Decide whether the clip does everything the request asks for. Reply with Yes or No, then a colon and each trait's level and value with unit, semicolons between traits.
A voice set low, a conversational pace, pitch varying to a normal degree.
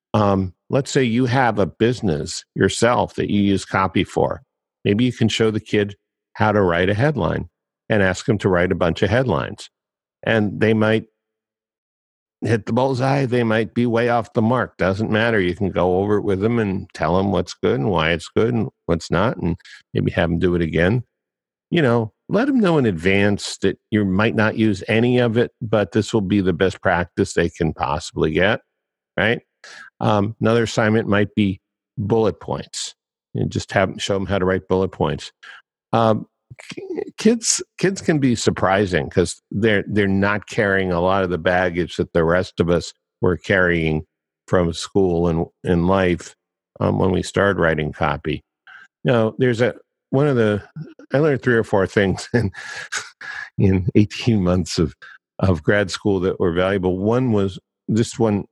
Yes: low, 105 Hz; average, 185 wpm; average, 3.9 semitones